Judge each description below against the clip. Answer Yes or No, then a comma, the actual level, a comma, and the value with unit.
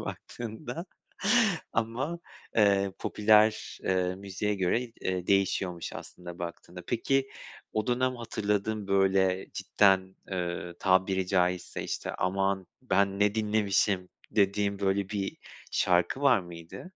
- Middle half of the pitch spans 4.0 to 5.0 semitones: No, average, 2.7 semitones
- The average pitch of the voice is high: No, low, 100 Hz